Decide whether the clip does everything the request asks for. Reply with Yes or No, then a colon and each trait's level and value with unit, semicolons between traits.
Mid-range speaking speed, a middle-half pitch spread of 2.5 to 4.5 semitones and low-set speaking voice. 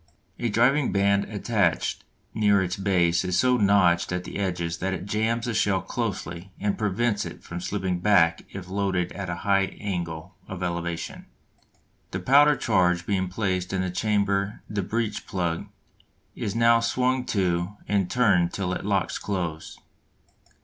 Yes: average, 155 wpm; average, 2.8 semitones; very low, 95 Hz